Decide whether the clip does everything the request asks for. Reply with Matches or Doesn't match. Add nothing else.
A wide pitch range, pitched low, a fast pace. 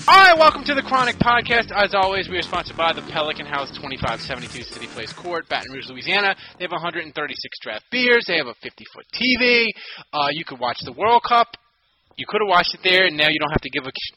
Doesn't match